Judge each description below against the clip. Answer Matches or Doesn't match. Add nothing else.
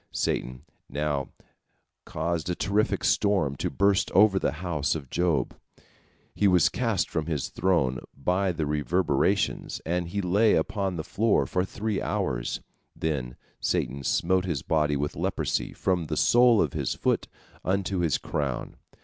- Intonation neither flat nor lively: Matches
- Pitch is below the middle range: Matches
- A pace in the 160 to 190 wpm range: Doesn't match